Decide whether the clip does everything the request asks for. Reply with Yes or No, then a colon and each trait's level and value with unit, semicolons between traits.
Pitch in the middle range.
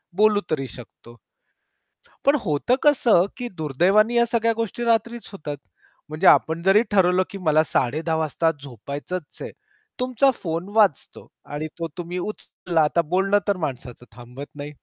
Yes: medium, 175 Hz